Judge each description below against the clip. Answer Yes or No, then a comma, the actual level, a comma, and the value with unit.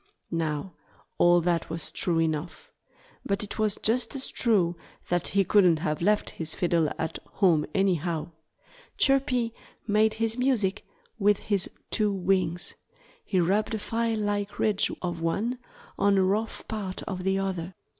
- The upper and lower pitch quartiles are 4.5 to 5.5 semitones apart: No, average, 3.7 semitones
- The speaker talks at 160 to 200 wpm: No, average, 150 wpm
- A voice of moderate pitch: No, high, 195 Hz